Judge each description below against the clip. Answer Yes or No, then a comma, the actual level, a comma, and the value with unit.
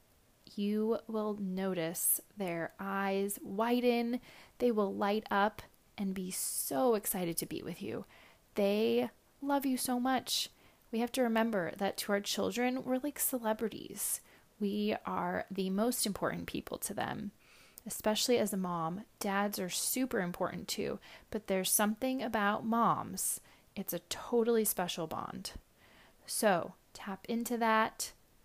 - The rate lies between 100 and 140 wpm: Yes, slow, 135 wpm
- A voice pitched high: Yes, high, 210 Hz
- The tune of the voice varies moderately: Yes, average, 3.3 semitones